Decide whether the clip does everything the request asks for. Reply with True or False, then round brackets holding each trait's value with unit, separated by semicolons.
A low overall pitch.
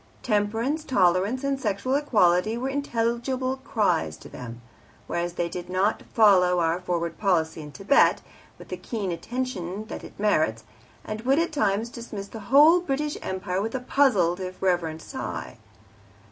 False (205 Hz)